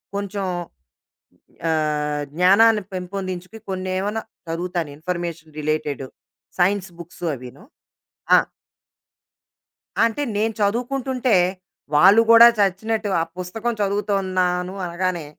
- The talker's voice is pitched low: No, medium, 185 Hz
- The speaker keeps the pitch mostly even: No, average, 3.4 semitones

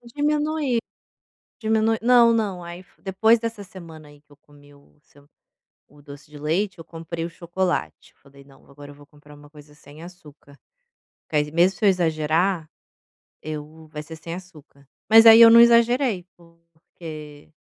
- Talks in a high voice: No, medium, 165 Hz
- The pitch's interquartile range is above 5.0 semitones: Yes, wide, 5.5 semitones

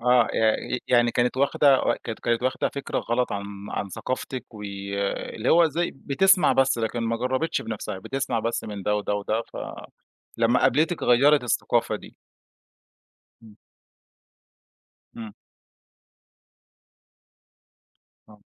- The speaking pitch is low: Yes, low, 120 Hz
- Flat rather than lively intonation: No, average, 3.5 semitones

